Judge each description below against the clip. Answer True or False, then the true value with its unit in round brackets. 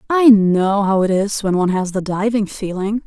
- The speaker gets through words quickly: True (215 wpm)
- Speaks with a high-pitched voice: True (200 Hz)